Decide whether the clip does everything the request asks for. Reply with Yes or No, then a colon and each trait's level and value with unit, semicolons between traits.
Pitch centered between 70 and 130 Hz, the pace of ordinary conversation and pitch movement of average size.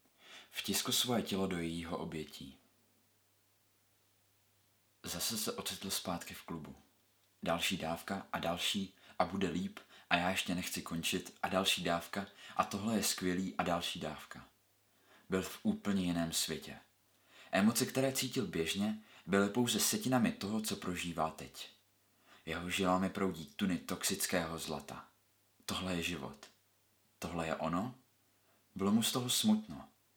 Yes: low, 100 Hz; average, 135 wpm; average, 3.9 semitones